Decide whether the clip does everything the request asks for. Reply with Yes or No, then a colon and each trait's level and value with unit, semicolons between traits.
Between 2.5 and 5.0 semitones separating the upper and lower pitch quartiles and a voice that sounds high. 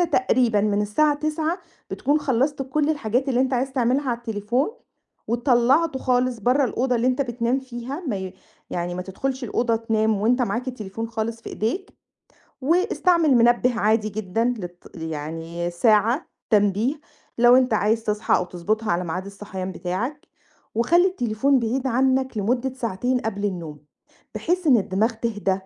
Yes: average, 4.1 semitones; high, 235 Hz